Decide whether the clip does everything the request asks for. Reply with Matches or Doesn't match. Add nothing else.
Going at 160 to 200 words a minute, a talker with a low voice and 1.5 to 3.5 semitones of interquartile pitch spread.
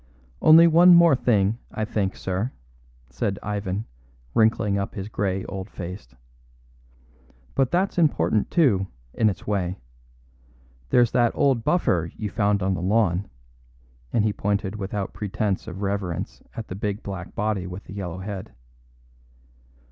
Doesn't match